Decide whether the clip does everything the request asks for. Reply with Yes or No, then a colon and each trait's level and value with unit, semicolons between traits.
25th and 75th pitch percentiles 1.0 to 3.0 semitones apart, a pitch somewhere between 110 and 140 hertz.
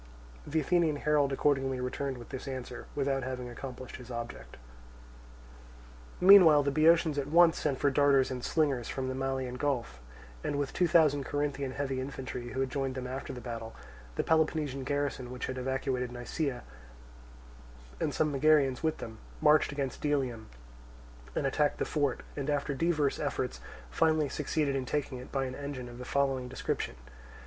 Yes: narrow, 2.4 semitones; low, 135 Hz